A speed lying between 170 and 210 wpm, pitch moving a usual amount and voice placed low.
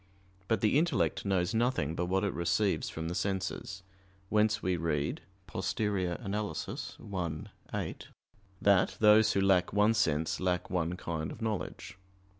No: average, 140 wpm; average, 3.4 semitones; very low, 95 Hz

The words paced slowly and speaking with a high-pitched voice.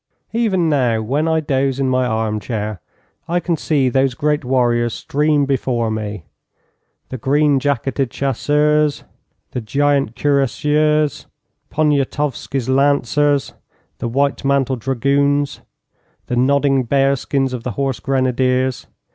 No: slow, 120 wpm; low, 135 Hz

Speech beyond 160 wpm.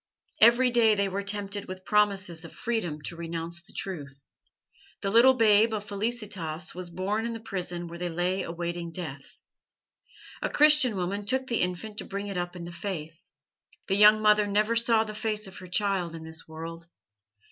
Yes: average, 185 wpm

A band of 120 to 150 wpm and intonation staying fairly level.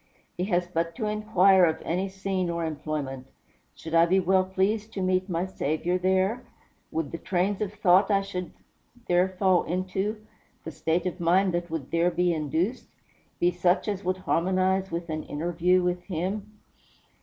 No: average, 170 wpm; narrow, 2.2 semitones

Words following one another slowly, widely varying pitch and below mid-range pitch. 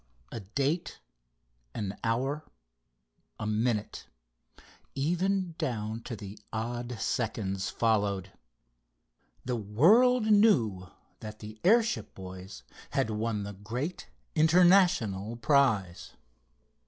Yes: slow, 90 wpm; wide, 6.9 semitones; low, 115 Hz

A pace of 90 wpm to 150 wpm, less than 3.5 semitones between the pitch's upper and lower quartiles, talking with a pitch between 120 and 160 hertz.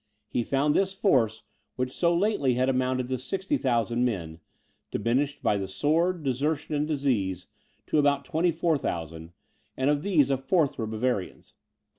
No: average, 145 wpm; average, 4.3 semitones; low, 135 Hz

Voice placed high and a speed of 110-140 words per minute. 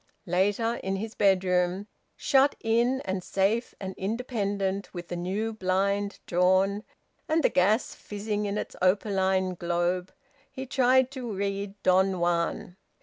Yes: high, 195 Hz; slow, 135 wpm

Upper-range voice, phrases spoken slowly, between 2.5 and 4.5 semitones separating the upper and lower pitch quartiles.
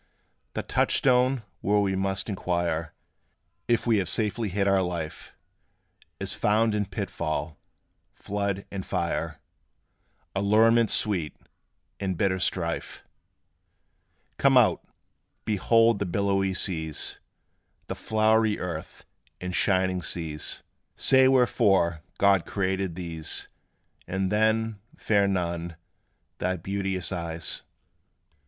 No: very low, 95 Hz; slow, 105 wpm; average, 3.2 semitones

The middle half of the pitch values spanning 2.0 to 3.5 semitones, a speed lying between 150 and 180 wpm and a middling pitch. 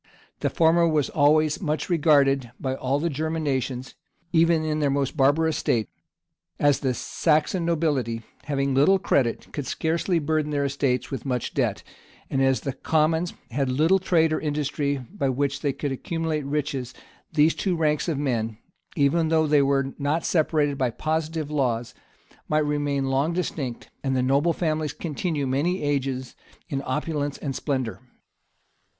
Yes: average, 2.8 semitones; average, 160 wpm; medium, 145 Hz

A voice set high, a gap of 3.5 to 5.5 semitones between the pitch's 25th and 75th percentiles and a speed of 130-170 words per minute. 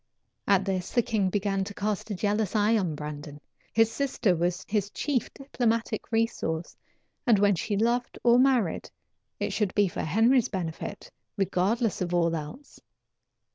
Yes: high, 205 Hz; average, 4.1 semitones; average, 155 wpm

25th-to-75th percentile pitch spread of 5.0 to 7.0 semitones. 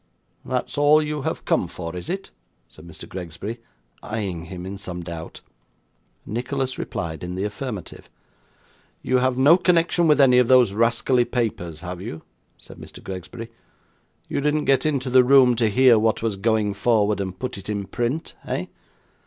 Yes: wide, 5.4 semitones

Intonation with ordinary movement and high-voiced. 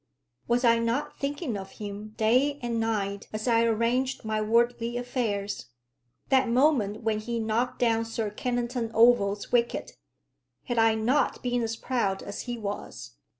No: narrow, 2.2 semitones; high, 230 Hz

